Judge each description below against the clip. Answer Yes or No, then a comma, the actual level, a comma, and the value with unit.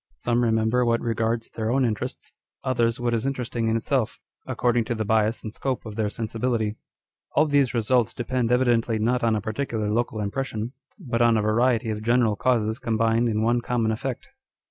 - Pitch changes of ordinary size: No, narrow, 1.8 semitones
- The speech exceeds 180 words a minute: Yes, average, 190 wpm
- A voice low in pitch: Yes, low, 115 Hz